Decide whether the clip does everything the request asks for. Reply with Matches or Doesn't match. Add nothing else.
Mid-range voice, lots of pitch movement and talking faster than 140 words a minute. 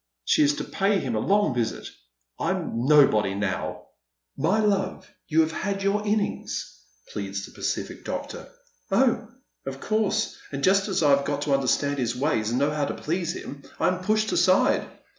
Matches